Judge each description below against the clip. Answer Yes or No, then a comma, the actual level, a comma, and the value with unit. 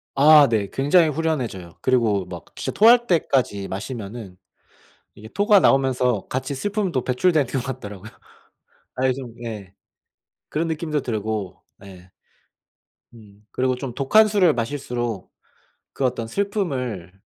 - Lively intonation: Yes, wide, 5.9 semitones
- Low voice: Yes, low, 125 Hz